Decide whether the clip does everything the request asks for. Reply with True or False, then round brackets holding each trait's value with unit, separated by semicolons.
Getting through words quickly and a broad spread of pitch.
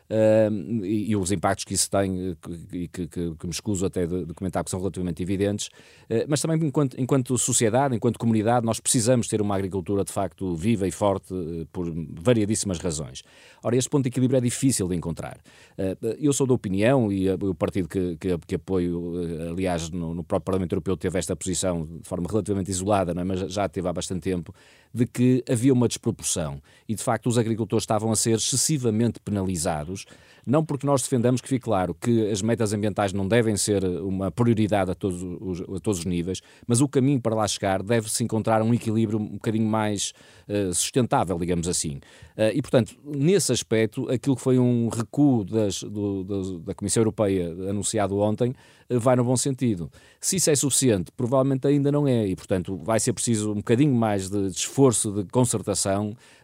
False (195 wpm; 4.4 semitones)